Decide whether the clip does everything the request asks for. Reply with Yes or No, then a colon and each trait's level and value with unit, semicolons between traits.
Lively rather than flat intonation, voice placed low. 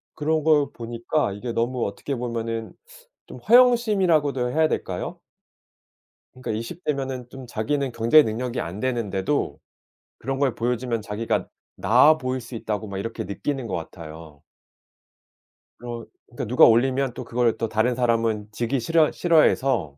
No: average, 3.6 semitones; low, 120 Hz